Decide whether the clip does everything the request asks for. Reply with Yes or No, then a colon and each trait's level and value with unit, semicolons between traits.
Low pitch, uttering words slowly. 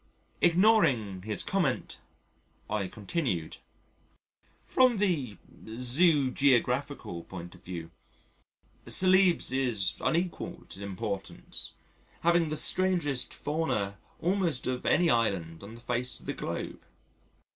Yes: low, 130 Hz; slow, 105 wpm